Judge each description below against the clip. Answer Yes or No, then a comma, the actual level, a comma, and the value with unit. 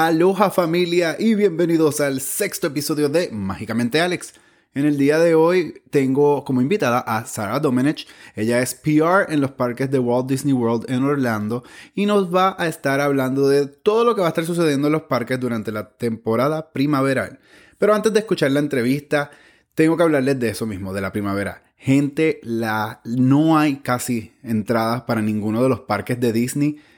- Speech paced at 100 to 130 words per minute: No, average, 180 wpm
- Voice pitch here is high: No, medium, 140 Hz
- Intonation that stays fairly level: No, average, 5.0 semitones